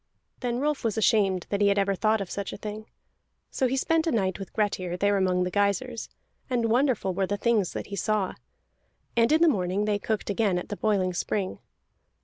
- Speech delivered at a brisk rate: Yes, fast, 210 wpm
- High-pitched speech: Yes, high, 205 Hz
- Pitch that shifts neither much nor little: Yes, average, 3.1 semitones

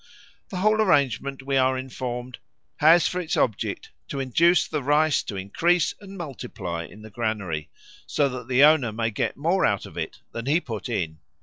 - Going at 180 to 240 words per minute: Yes, average, 185 wpm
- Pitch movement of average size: No, wide, 5.9 semitones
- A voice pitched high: No, low, 130 Hz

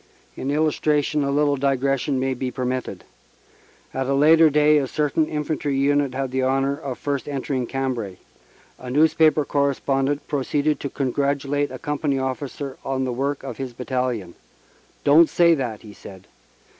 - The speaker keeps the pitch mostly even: Yes, narrow, 2.0 semitones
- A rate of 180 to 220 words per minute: No, average, 160 wpm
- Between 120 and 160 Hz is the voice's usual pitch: Yes, medium, 140 Hz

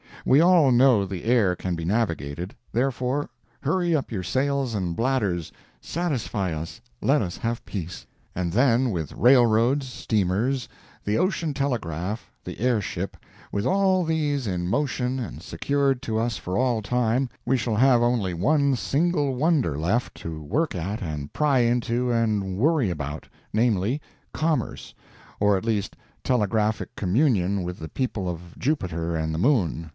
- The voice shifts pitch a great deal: Yes, wide, 6.4 semitones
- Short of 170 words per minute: Yes, average, 140 wpm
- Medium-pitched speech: No, low, 115 Hz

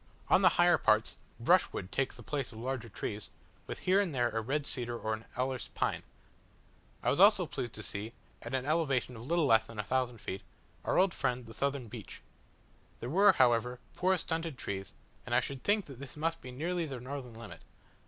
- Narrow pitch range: No, average, 4.2 semitones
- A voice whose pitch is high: No, low, 125 Hz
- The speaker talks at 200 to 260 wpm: Yes, fast, 205 wpm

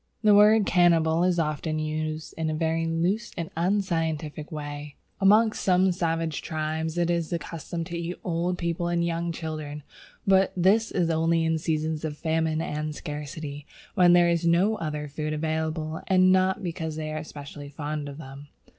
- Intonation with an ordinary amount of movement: No, narrow, 2.1 semitones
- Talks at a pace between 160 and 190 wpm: Yes, average, 175 wpm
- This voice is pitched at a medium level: Yes, medium, 165 Hz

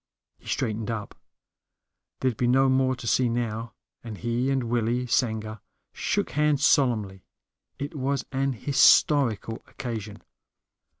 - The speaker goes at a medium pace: No, slow, 125 wpm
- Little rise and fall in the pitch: No, average, 3.1 semitones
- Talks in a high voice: No, low, 120 Hz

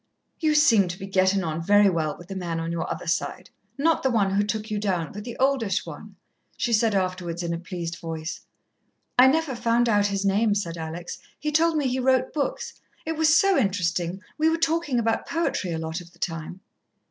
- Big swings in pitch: Yes, wide, 6.9 semitones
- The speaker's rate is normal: No, fast, 215 wpm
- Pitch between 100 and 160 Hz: No, high, 200 Hz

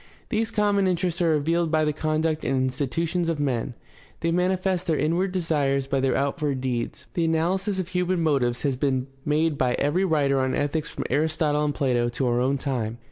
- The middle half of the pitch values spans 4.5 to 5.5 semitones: No, average, 4.0 semitones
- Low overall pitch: No, medium, 155 Hz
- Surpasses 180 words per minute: Yes, average, 190 wpm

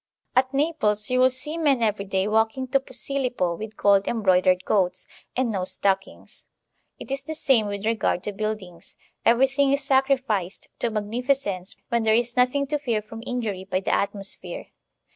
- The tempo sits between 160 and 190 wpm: Yes, average, 170 wpm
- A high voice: Yes, high, 225 Hz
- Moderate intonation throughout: Yes, average, 4.8 semitones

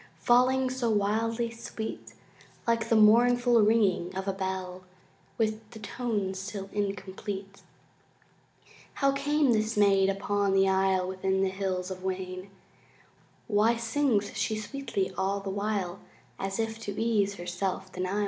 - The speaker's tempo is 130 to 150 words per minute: Yes, average, 140 wpm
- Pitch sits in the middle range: No, high, 205 Hz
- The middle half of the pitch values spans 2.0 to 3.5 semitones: Yes, average, 2.9 semitones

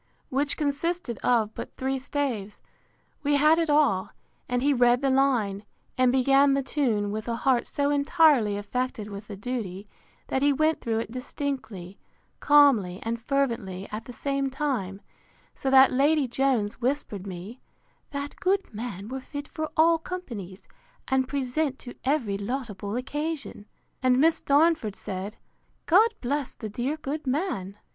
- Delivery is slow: No, average, 155 wpm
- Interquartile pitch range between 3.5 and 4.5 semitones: No, average, 5.1 semitones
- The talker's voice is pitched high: Yes, very high, 260 Hz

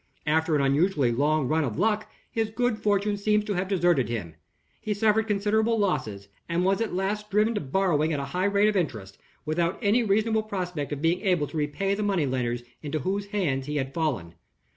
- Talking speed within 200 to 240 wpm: Yes, fast, 205 wpm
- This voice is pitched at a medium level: Yes, medium, 180 Hz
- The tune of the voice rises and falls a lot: Yes, wide, 6.1 semitones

